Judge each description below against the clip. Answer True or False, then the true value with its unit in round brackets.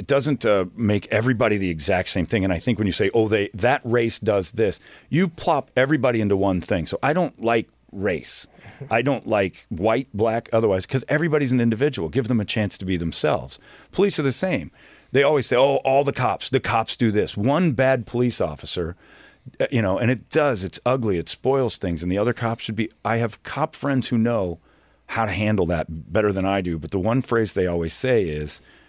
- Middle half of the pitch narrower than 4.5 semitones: False (5.3 semitones)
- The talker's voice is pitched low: True (115 Hz)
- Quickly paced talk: True (220 wpm)